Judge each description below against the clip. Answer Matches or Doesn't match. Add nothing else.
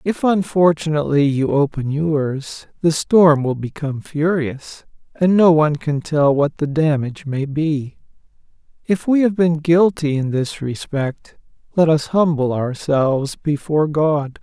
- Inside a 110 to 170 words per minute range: Matches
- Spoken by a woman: Doesn't match